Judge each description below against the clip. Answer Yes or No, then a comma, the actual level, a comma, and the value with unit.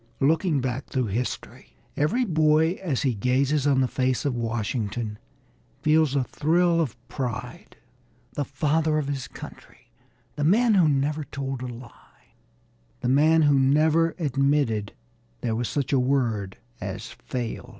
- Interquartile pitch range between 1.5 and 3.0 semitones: No, average, 3.6 semitones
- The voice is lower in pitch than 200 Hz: Yes, medium, 140 Hz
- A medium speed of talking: Yes, average, 145 wpm